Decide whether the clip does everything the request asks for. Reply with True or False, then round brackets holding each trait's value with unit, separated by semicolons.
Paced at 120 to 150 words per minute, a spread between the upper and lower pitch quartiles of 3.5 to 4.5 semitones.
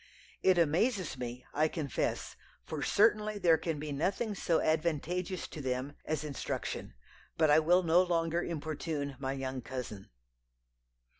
True (140 wpm; 3.9 semitones)